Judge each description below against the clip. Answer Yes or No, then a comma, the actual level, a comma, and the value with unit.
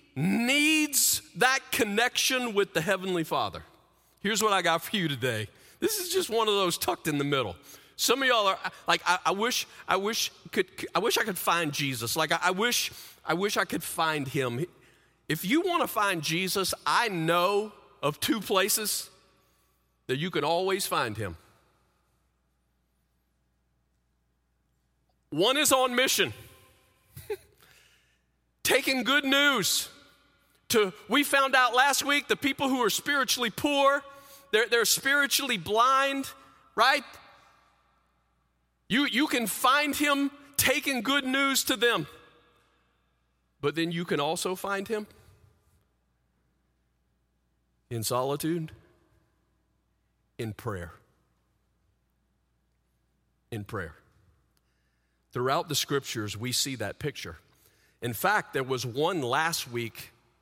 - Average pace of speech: No, slow, 130 wpm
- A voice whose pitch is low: No, medium, 155 Hz